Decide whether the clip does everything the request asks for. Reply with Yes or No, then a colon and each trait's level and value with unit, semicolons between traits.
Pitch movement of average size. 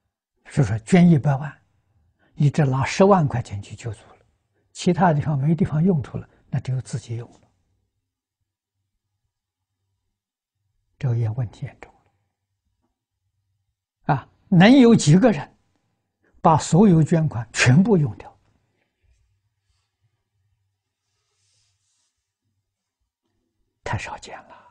No: wide, 6.1 semitones